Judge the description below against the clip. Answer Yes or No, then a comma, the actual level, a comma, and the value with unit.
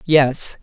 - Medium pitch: Yes, medium, 145 Hz